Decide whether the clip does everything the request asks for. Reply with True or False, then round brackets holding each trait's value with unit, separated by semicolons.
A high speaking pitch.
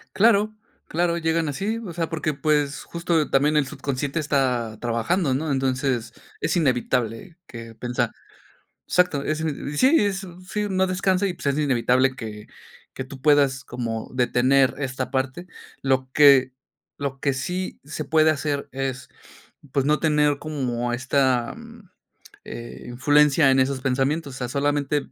False (140 Hz)